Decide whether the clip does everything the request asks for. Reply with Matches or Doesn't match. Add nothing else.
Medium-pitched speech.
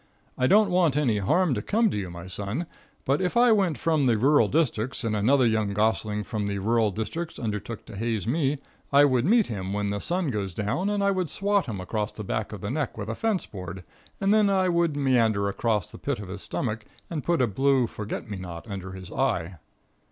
Doesn't match